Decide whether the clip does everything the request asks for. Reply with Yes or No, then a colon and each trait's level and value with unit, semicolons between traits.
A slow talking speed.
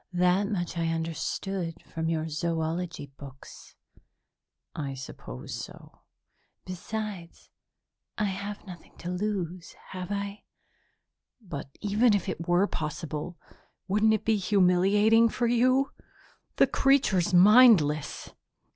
Yes: slow, 110 wpm